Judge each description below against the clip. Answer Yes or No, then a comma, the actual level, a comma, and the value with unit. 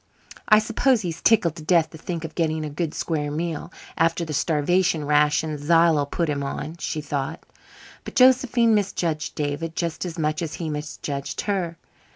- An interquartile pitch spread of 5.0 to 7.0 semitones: No, narrow, 2.5 semitones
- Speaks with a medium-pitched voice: Yes, medium, 160 Hz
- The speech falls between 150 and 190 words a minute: Yes, average, 175 wpm